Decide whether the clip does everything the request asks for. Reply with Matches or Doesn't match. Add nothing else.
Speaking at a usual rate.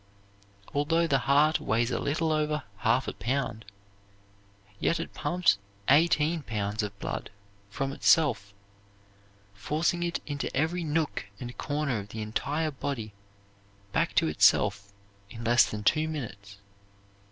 Doesn't match